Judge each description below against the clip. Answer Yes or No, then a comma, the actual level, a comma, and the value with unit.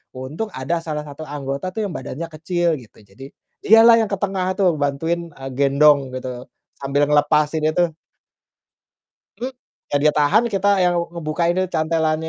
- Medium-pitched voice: Yes, medium, 155 Hz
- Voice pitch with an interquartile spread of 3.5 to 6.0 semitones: Yes, average, 3.9 semitones